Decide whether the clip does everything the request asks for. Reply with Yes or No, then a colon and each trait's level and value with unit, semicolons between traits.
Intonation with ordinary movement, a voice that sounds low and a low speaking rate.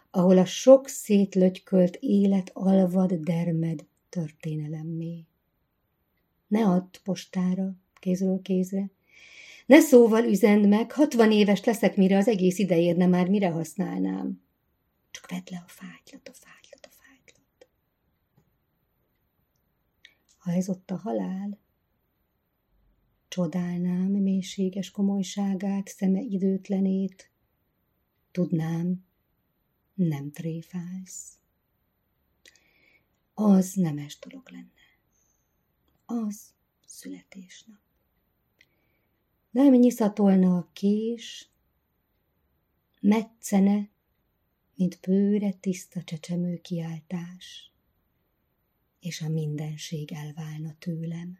No: average, 3.0 semitones; medium, 185 Hz; slow, 85 wpm